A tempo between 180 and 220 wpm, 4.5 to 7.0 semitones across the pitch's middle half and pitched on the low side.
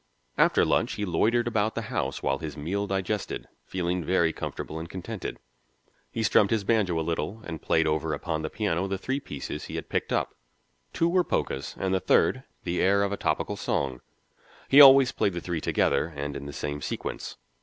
Yes: average, 195 wpm; average, 4.9 semitones; very low, 90 Hz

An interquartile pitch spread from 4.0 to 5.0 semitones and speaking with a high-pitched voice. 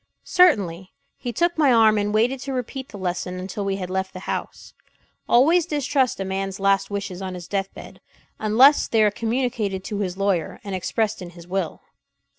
Yes: average, 4.3 semitones; high, 200 Hz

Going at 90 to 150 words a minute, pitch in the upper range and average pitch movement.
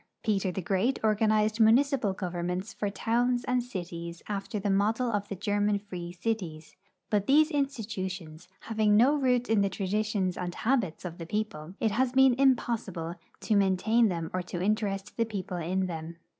No: average, 170 wpm; high, 205 Hz; average, 3.9 semitones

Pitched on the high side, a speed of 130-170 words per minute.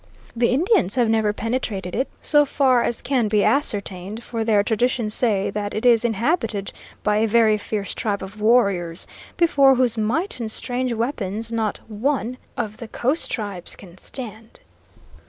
Yes: high, 225 Hz; average, 160 wpm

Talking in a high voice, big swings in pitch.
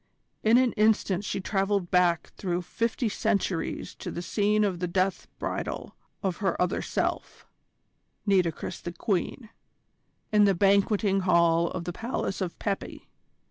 No: high, 195 Hz; average, 2.9 semitones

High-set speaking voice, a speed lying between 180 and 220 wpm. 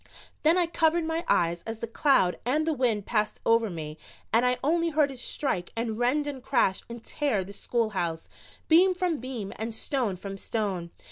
Yes: high, 235 Hz; average, 190 wpm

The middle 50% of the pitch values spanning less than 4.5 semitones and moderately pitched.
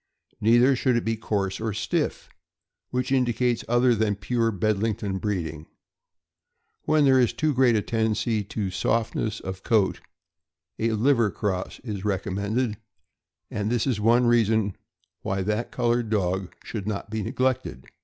No: average, 2.9 semitones; low, 110 Hz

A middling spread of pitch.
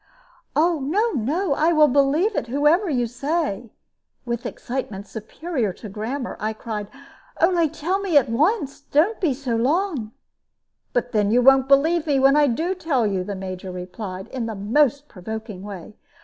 No: wide, 6.2 semitones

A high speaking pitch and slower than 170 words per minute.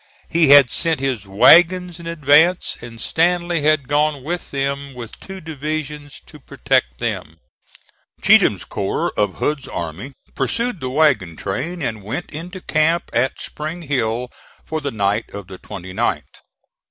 No: medium, 145 Hz; average, 145 wpm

